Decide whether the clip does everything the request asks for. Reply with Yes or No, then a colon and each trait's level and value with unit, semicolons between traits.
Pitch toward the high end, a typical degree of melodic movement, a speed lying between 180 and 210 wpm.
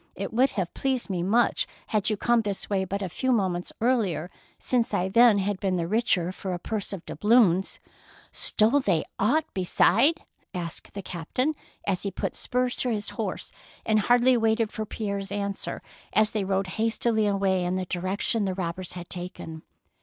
Yes: high, 200 Hz; average, 3.5 semitones; average, 190 wpm